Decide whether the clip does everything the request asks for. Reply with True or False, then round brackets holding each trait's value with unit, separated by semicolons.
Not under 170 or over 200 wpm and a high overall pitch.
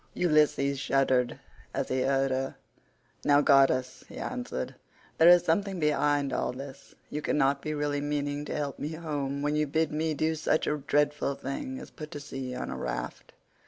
False (180 wpm; 145 Hz)